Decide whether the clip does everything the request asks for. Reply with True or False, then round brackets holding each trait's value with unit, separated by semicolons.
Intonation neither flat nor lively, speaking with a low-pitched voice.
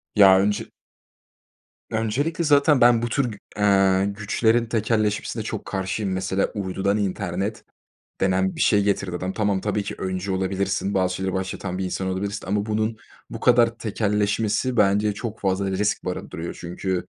False (2.3 semitones; 100 Hz)